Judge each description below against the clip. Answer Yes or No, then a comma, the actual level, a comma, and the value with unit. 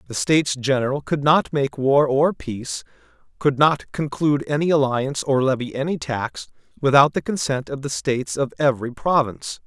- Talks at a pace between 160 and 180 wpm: Yes, average, 170 wpm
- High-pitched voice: No, low, 135 Hz